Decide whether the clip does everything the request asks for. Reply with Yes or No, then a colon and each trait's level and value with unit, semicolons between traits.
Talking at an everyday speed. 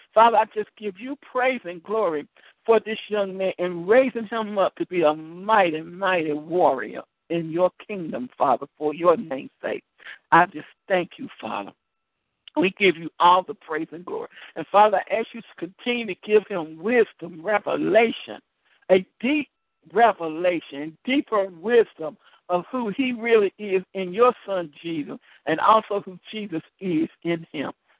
Yes: average, 165 wpm